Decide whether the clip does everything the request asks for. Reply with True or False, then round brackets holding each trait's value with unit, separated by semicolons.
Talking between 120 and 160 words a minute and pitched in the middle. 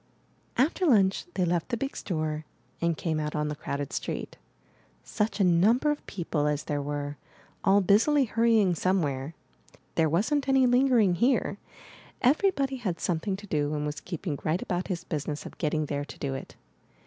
False (175 wpm; 175 Hz)